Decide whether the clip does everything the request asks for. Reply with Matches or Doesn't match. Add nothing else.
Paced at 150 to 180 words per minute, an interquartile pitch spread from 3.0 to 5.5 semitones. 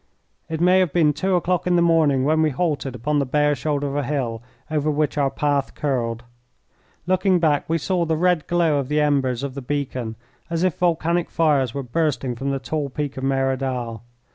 Doesn't match